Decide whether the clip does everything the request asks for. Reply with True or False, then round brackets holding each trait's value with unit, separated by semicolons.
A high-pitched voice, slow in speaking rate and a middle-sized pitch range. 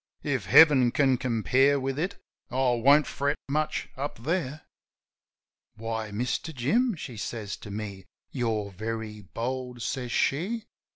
False (125 Hz; 130 wpm; 4.1 semitones)